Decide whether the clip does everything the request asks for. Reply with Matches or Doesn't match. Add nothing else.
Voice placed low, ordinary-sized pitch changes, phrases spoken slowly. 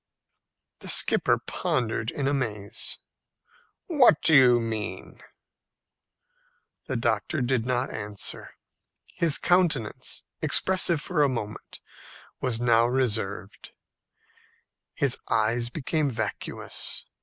Matches